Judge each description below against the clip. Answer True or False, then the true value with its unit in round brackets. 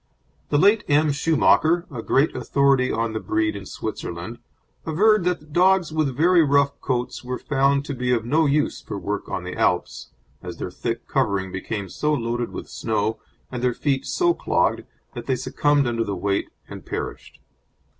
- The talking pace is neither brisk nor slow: True (175 wpm)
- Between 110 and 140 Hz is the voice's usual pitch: True (135 Hz)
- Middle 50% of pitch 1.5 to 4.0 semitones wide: False (5.0 semitones)